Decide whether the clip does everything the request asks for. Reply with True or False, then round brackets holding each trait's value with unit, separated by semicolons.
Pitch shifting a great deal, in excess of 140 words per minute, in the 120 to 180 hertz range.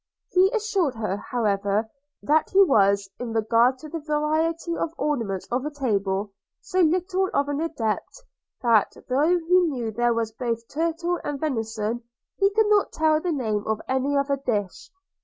False (6.8 semitones; 165 wpm; 275 Hz)